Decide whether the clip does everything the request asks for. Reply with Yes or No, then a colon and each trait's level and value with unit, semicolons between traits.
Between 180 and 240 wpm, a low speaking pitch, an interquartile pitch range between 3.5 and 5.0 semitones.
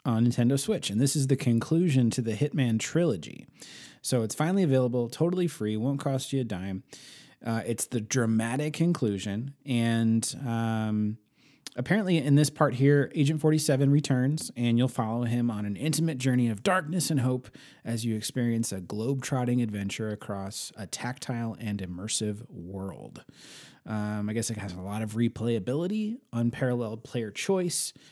No: average, 160 wpm; low, 120 Hz; average, 4.4 semitones